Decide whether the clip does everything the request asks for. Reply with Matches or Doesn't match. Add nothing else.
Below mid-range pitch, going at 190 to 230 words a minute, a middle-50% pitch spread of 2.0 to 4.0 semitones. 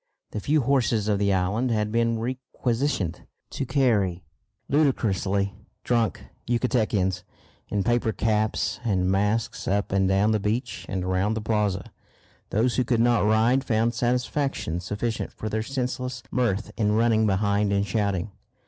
Doesn't match